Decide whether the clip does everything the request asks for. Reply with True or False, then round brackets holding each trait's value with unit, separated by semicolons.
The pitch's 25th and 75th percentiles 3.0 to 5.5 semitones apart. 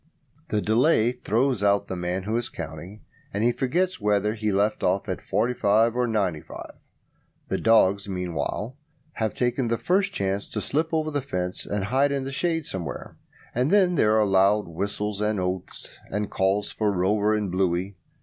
True (4.2 semitones)